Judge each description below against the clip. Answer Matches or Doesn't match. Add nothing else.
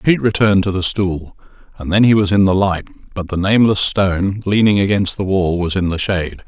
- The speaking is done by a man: Matches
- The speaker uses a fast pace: Matches